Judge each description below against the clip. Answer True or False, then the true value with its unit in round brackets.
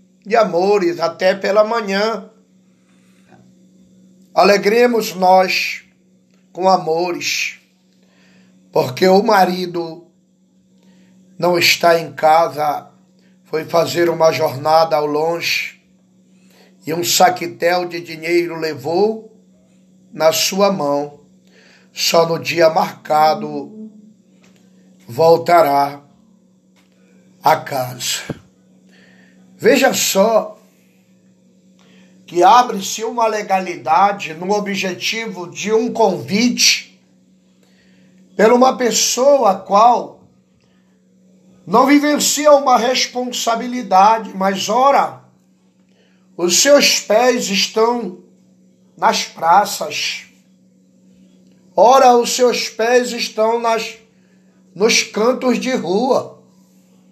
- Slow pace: True (80 wpm)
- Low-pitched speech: False (185 Hz)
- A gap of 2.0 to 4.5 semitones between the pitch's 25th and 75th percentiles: True (4.2 semitones)